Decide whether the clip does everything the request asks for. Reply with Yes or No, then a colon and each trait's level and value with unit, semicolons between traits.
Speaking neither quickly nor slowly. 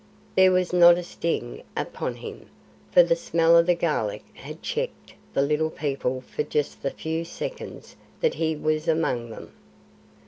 Yes: average, 165 wpm